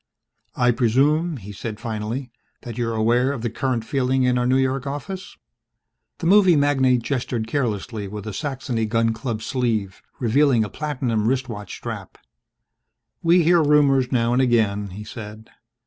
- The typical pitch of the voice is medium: No, low, 125 Hz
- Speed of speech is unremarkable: Yes, average, 155 wpm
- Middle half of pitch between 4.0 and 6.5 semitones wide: No, average, 3.6 semitones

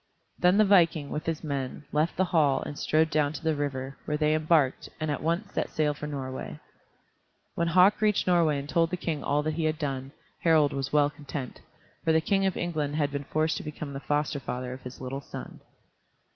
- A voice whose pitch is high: No, medium, 150 Hz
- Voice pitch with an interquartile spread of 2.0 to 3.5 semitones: Yes, narrow, 2.5 semitones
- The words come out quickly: Yes, fast, 215 wpm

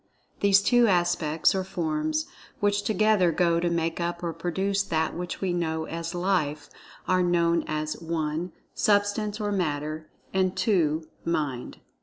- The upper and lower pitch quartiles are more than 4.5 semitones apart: No, average, 3.3 semitones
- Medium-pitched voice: Yes, medium, 175 Hz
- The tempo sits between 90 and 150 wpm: Yes, average, 145 wpm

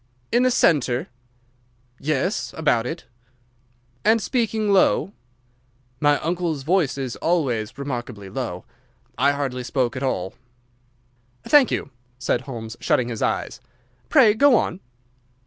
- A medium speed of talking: No, slow, 120 wpm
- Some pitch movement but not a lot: No, wide, 7.5 semitones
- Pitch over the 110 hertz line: Yes, medium, 140 Hz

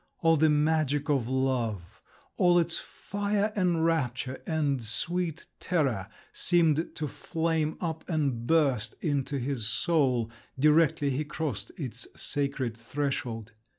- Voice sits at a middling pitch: Yes, medium, 145 Hz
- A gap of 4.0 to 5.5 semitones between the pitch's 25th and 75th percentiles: Yes, average, 4.3 semitones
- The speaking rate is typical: No, slow, 120 wpm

